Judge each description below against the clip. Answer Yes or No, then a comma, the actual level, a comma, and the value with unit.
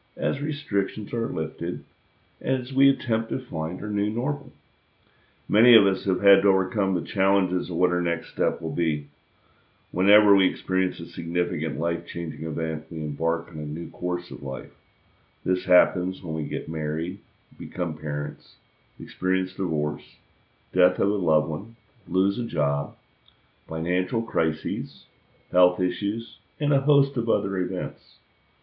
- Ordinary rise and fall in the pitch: Yes, average, 4.0 semitones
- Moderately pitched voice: No, very low, 90 Hz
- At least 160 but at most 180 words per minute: No, average, 150 wpm